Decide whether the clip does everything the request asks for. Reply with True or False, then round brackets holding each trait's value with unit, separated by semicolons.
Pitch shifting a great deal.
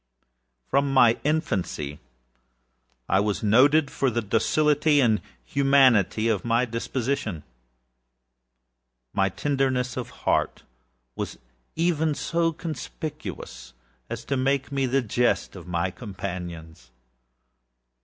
True (5.9 semitones)